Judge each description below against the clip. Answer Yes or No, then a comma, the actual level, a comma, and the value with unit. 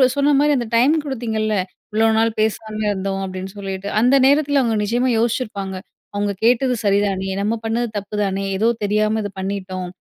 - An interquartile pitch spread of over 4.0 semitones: No, average, 3.3 semitones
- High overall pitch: Yes, high, 215 Hz